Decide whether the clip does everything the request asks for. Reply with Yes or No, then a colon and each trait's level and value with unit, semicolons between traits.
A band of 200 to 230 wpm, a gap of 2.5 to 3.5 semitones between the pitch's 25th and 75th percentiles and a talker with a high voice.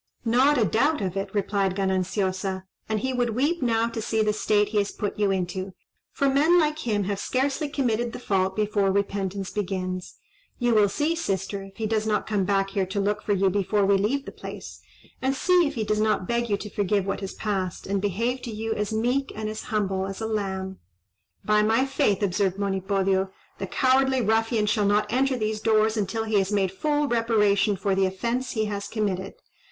Yes: fast, 205 wpm; average, 3.0 semitones; high, 210 Hz